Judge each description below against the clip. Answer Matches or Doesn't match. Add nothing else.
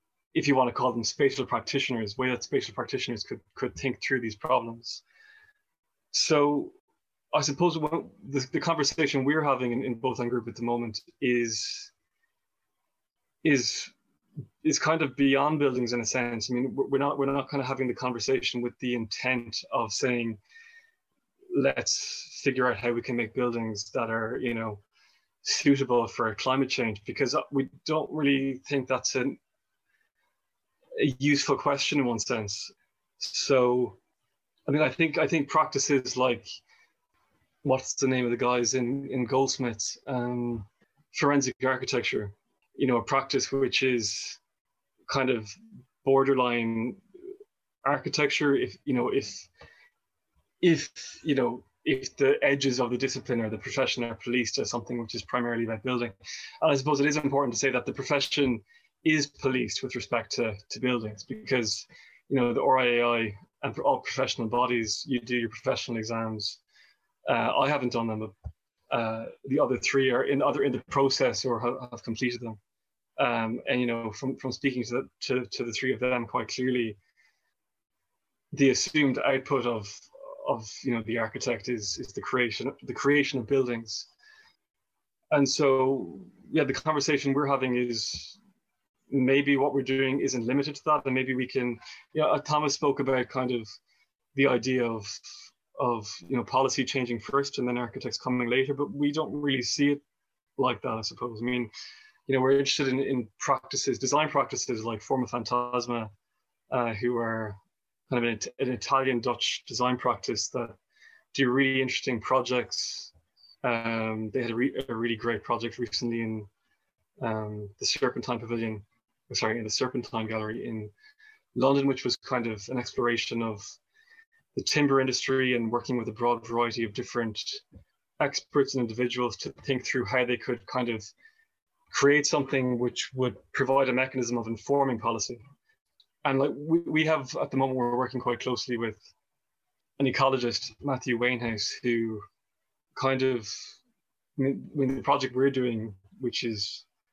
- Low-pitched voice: Matches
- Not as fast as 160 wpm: Doesn't match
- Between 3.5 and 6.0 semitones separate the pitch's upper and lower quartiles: Doesn't match